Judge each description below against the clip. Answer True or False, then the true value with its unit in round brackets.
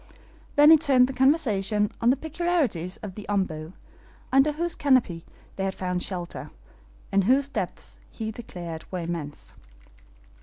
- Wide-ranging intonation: True (7.5 semitones)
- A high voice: True (210 Hz)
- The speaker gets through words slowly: False (145 wpm)